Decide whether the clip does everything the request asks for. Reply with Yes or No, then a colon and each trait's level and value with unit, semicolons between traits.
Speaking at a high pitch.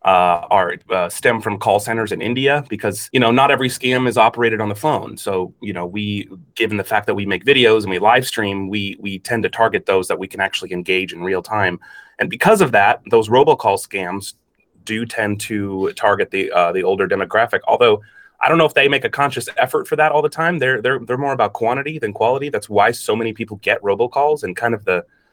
No: low, 115 Hz